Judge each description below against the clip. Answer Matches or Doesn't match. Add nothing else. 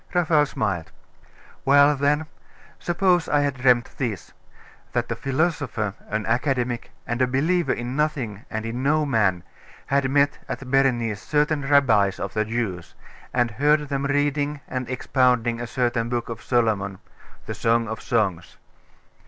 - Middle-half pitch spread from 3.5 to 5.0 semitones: Matches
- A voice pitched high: Doesn't match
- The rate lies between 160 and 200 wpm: Doesn't match